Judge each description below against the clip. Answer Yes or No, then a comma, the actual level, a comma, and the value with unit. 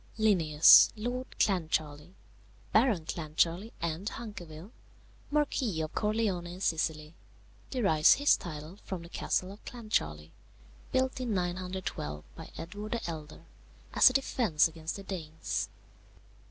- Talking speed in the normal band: No, slow, 120 wpm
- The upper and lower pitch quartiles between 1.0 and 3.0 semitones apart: No, average, 5.2 semitones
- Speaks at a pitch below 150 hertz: No, medium, 180 Hz